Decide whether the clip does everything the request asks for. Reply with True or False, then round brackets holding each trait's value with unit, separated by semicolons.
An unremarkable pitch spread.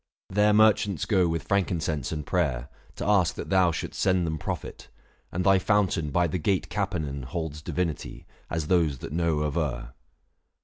True (3.9 semitones)